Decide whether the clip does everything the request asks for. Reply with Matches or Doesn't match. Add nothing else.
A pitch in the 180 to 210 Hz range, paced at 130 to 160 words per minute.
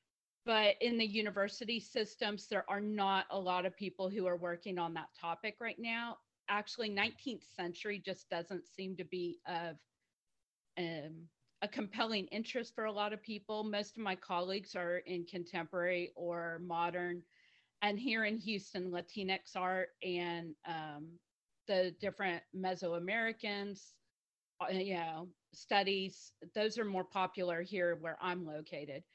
Matches